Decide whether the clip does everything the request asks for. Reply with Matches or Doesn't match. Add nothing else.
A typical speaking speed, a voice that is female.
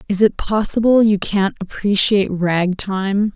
Matches